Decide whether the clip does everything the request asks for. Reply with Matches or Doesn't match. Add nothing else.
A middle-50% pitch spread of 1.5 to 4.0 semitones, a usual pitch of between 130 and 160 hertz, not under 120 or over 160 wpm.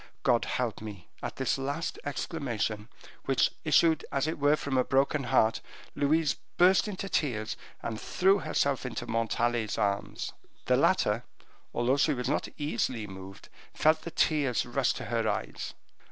Doesn't match